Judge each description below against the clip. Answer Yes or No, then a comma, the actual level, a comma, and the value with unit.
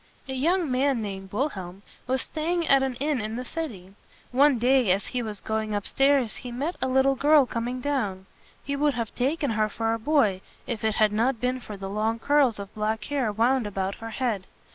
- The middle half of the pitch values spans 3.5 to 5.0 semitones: Yes, average, 4.3 semitones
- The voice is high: Yes, high, 245 Hz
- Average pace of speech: No, fast, 215 wpm